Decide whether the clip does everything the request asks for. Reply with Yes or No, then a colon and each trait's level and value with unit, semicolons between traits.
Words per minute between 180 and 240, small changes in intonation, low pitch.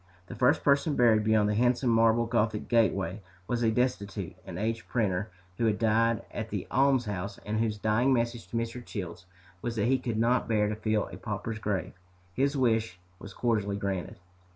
Yes: average, 185 wpm; narrow, 2.3 semitones; low, 110 Hz